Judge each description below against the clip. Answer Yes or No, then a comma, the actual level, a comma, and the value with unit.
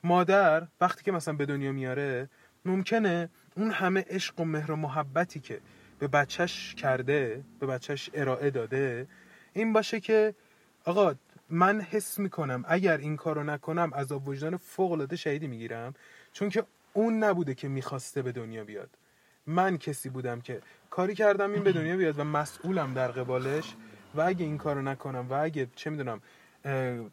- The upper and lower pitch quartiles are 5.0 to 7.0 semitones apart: Yes, wide, 5.4 semitones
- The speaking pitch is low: No, medium, 155 Hz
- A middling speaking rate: No, fast, 165 wpm